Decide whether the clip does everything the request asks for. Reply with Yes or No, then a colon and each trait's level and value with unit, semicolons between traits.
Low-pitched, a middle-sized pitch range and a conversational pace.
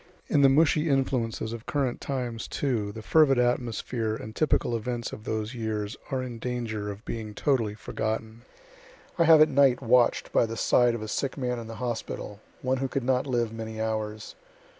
Yes: low, 120 Hz; average, 3.1 semitones; average, 185 wpm